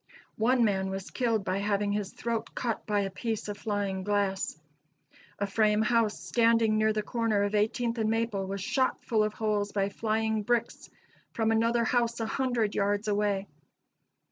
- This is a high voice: Yes, high, 215 Hz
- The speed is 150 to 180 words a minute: Yes, average, 170 wpm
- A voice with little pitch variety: Yes, narrow, 2.1 semitones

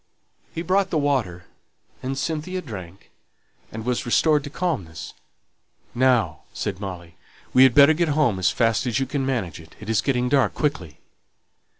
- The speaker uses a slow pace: No, average, 160 wpm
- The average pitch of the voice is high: No, low, 125 Hz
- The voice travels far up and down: Yes, wide, 6.3 semitones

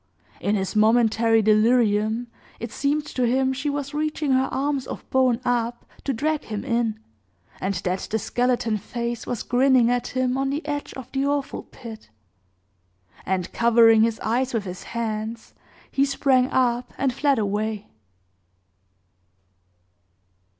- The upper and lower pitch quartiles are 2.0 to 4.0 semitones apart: Yes, average, 3.3 semitones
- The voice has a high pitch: Yes, high, 240 Hz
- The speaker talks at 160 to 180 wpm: No, average, 145 wpm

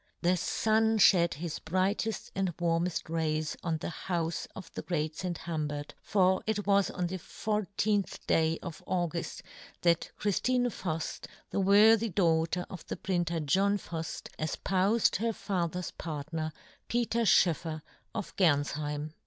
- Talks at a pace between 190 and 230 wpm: No, average, 140 wpm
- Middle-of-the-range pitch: Yes, medium, 175 Hz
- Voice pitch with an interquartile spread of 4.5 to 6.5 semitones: No, average, 3.7 semitones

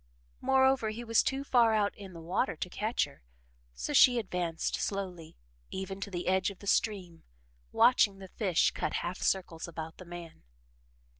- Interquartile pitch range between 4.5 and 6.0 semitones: No, average, 3.9 semitones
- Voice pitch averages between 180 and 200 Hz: Yes, high, 190 Hz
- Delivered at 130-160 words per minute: No, average, 170 wpm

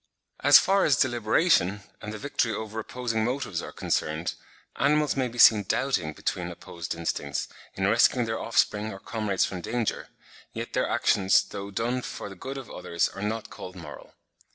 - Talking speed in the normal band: Yes, average, 175 wpm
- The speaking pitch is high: No, low, 110 Hz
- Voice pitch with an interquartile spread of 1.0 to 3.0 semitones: No, average, 4.2 semitones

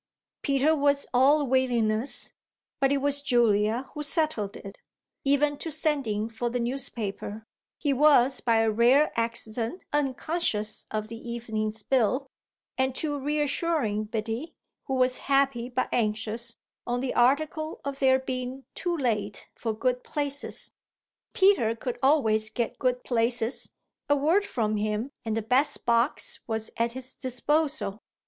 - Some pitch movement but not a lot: Yes, average, 4.0 semitones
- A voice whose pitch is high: Yes, very high, 250 Hz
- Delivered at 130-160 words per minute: Yes, average, 140 wpm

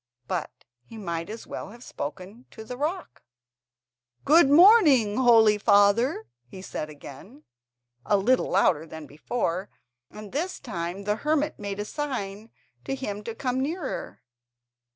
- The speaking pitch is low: No, high, 220 Hz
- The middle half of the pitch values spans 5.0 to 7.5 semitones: Yes, wide, 5.4 semitones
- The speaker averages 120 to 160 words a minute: Yes, average, 140 wpm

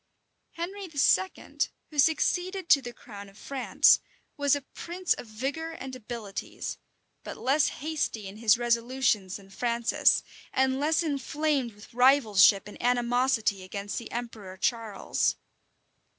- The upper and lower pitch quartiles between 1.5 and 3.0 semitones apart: No, average, 5.0 semitones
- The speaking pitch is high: Yes, high, 245 Hz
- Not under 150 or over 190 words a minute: No, slow, 135 wpm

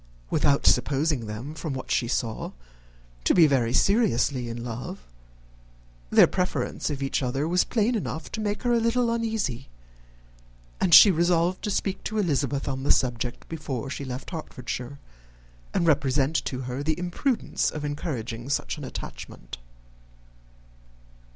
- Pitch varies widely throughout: Yes, wide, 6.1 semitones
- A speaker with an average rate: Yes, average, 145 wpm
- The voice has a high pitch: No, medium, 145 Hz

